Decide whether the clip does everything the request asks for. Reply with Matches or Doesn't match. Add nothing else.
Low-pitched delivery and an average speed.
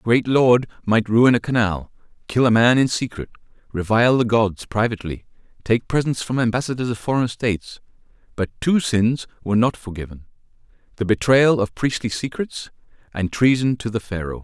Matches